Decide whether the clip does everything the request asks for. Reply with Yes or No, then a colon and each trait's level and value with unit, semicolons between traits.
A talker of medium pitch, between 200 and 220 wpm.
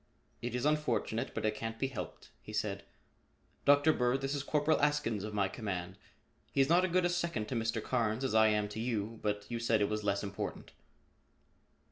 No: low, 115 Hz; fast, 205 wpm